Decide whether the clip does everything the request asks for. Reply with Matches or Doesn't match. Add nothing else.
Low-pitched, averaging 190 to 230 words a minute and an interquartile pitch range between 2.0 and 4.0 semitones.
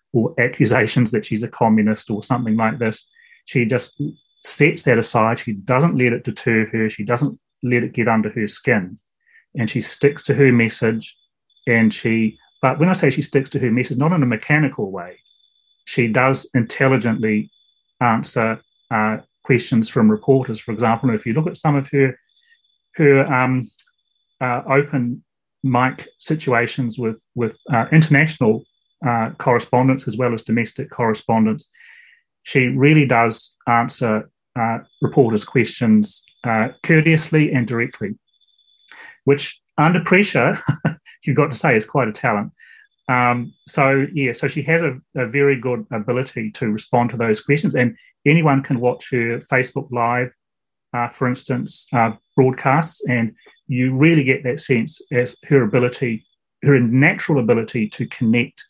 Doesn't match